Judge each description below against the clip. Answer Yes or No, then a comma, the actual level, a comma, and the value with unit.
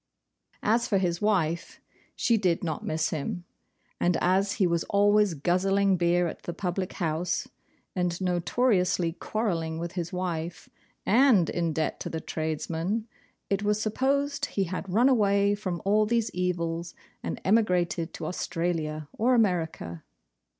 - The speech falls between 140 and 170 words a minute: Yes, average, 145 wpm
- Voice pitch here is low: No, medium, 180 Hz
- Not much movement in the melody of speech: No, average, 3.5 semitones